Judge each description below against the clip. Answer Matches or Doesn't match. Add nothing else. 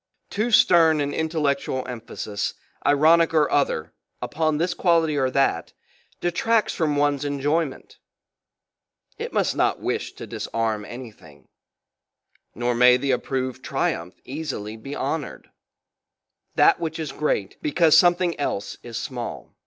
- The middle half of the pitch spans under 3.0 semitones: Doesn't match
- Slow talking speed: Matches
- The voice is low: Doesn't match